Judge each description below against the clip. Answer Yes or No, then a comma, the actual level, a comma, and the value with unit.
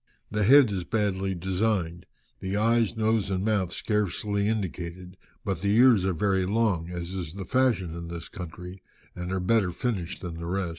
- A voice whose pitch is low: Yes, very low, 95 Hz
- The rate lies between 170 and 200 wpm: Yes, average, 180 wpm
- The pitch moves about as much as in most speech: Yes, average, 3.2 semitones